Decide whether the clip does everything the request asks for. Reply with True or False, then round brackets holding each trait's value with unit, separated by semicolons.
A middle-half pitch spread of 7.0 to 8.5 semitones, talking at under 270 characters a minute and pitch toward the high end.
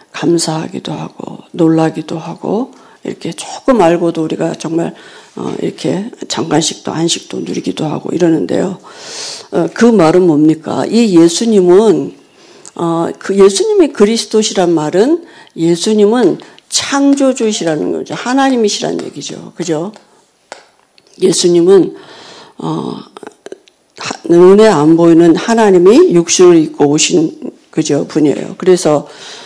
True (8.2 semitones; 260 characters per minute; 195 Hz)